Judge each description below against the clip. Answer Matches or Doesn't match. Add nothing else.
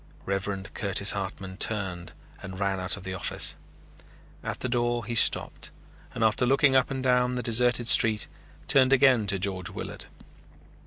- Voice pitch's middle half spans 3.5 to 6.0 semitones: Matches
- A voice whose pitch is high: Doesn't match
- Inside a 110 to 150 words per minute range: Doesn't match